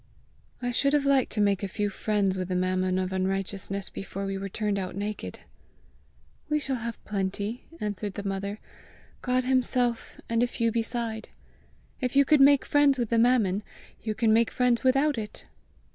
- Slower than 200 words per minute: Yes, average, 180 wpm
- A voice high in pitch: Yes, high, 220 Hz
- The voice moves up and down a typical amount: Yes, average, 4.2 semitones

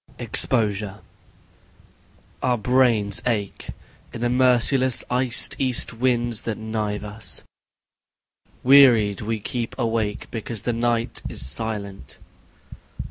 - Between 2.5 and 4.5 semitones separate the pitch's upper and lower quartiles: Yes, average, 2.8 semitones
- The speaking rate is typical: No, slow, 105 wpm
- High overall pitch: No, low, 115 Hz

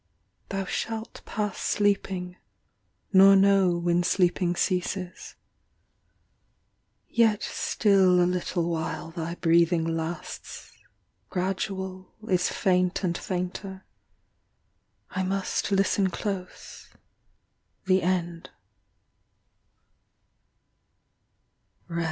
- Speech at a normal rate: No, slow, 75 wpm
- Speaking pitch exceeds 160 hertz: Yes, medium, 185 Hz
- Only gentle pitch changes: Yes, narrow, 1.8 semitones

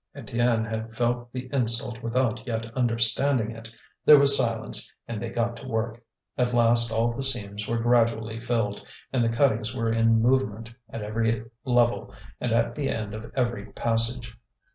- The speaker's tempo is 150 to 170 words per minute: Yes, average, 165 wpm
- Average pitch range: No, narrow, 1.3 semitones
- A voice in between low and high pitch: No, low, 115 Hz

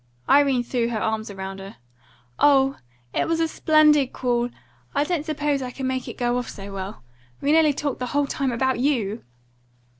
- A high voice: Yes, very high, 260 Hz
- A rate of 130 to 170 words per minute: No, average, 185 wpm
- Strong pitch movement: No, average, 3.7 semitones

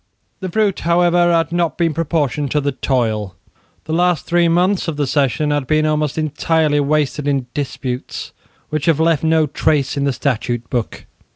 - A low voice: No, medium, 150 Hz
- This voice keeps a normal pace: Yes, average, 175 wpm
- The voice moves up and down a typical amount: Yes, average, 3.1 semitones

